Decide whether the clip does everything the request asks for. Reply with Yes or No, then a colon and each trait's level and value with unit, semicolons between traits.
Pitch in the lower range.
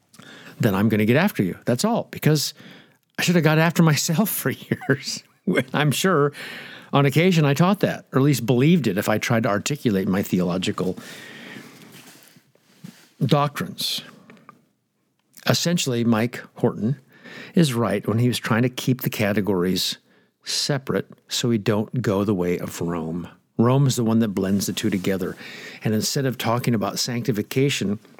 Yes: low, 130 Hz